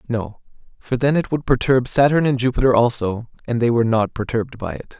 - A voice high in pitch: No, low, 120 Hz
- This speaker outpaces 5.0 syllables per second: Yes, 5.8 syllables/s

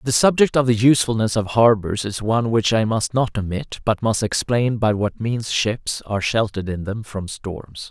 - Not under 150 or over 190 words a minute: No, fast, 205 wpm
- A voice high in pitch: No, low, 110 Hz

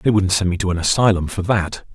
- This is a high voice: No, very low, 95 Hz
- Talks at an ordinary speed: No, fast, 280 wpm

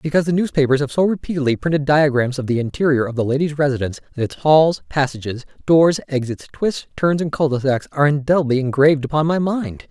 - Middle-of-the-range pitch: Yes, medium, 145 Hz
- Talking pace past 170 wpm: Yes, average, 200 wpm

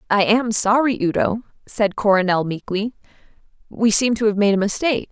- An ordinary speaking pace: Yes, average, 165 wpm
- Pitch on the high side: Yes, high, 210 Hz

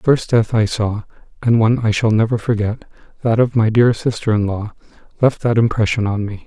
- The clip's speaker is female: No, male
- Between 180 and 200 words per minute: Yes, average, 195 wpm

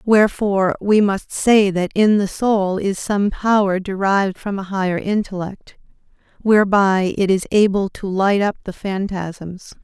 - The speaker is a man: No, female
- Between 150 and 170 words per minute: Yes, average, 155 wpm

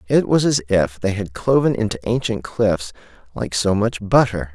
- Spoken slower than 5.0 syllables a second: Yes, 4.7 syllables/s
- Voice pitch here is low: Yes, low, 105 Hz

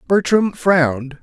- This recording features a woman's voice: No, male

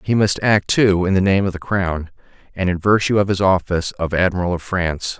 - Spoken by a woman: No, male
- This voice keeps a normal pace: No, fast, 230 wpm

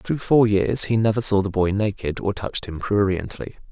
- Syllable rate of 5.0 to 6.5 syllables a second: Yes, 5.1 syllables/s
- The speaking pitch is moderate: No, low, 100 Hz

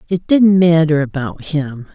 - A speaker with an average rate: Yes, average, 155 wpm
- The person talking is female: Yes, female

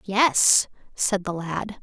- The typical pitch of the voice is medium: No, high, 195 Hz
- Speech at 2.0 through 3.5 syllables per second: Yes, 2.8 syllables/s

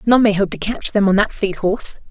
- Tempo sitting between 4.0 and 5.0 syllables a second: No, 5.7 syllables/s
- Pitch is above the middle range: Yes, high, 205 Hz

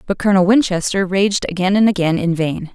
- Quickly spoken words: No, average, 195 wpm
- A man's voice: No, female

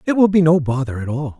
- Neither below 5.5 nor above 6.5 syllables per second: Yes, 6.4 syllables/s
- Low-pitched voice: No, medium, 150 Hz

